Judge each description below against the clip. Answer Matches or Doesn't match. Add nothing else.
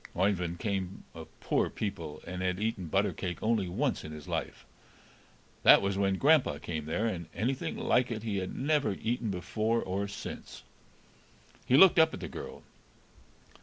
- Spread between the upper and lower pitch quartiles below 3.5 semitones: Doesn't match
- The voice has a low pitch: Matches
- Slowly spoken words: Doesn't match